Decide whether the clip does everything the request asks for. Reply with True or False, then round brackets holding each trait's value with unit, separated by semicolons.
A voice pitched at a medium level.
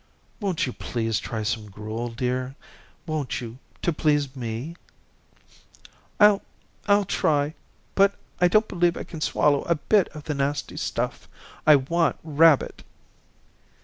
True (145 Hz)